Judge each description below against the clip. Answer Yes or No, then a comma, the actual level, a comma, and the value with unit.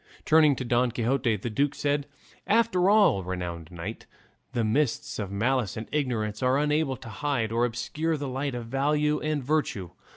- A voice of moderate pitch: No, low, 130 Hz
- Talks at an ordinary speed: Yes, average, 170 wpm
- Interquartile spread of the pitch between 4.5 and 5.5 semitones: Yes, average, 5.0 semitones